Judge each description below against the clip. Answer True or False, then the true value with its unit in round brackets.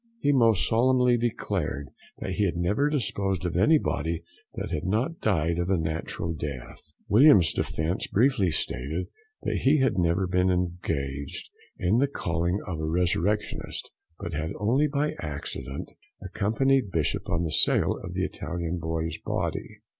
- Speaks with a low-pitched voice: True (90 Hz)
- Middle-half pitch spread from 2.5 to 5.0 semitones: False (5.6 semitones)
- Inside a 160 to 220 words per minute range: False (150 wpm)